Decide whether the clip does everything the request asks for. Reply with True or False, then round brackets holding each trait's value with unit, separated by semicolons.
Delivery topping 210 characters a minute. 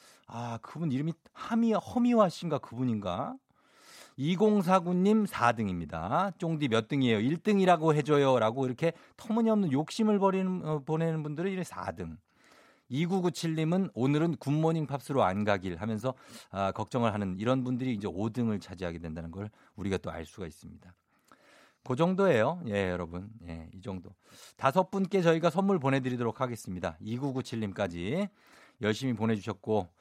True (320 characters per minute)